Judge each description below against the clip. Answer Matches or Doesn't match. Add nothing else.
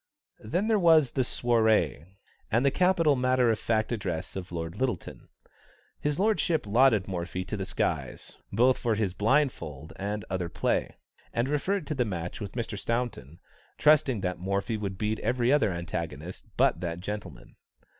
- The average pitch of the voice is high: Doesn't match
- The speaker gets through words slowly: Doesn't match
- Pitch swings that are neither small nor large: Doesn't match